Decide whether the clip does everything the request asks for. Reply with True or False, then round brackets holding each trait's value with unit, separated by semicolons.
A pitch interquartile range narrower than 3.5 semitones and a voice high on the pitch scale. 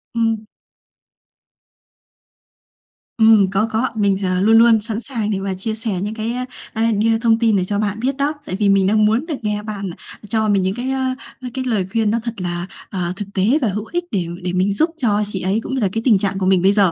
True (2.7 semitones; 215 Hz)